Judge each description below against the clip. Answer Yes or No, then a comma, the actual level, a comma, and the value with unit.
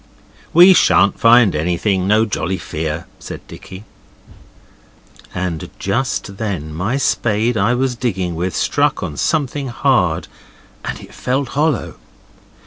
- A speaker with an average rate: No, slow, 125 wpm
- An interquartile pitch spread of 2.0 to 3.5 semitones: No, wide, 5.5 semitones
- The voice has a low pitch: Yes, low, 105 Hz